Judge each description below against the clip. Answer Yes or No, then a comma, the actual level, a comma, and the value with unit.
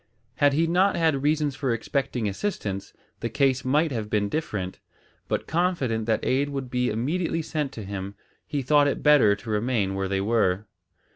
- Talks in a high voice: No, low, 130 Hz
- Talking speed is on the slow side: No, average, 180 wpm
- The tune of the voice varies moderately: No, wide, 5.9 semitones